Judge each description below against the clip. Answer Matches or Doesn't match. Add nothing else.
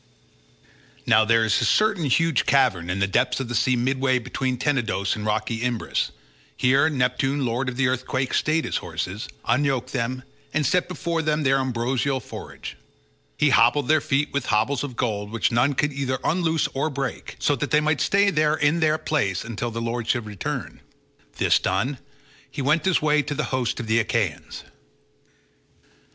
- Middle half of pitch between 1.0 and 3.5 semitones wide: Doesn't match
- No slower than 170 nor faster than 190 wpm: Matches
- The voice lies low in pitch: Matches